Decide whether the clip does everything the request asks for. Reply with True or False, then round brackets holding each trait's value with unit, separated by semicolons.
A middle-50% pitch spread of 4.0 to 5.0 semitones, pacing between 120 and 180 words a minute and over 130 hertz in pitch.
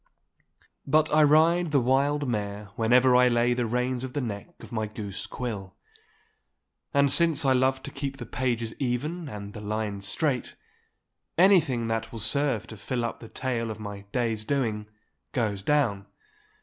False (4.3 semitones; 165 wpm; 125 Hz)